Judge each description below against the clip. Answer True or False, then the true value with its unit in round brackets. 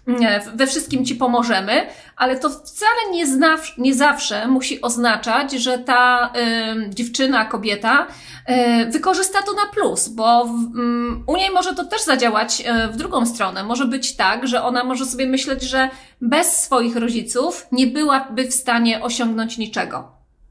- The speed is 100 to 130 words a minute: False (160 wpm)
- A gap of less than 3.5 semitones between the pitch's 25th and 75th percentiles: True (3.1 semitones)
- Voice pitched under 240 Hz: False (255 Hz)